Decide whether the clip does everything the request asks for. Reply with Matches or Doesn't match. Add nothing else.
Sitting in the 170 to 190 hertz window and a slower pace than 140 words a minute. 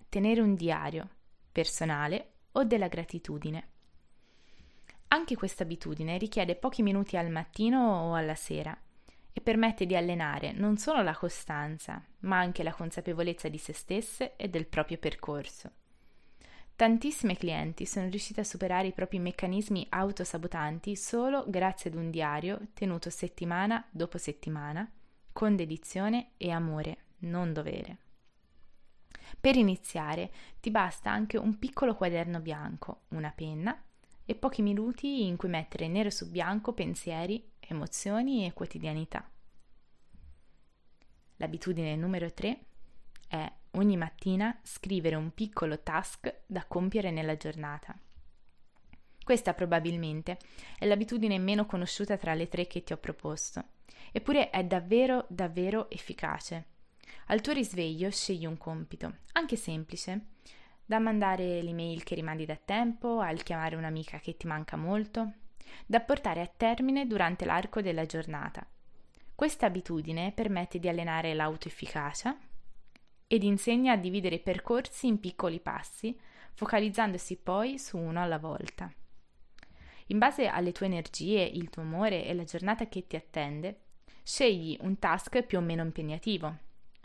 Matches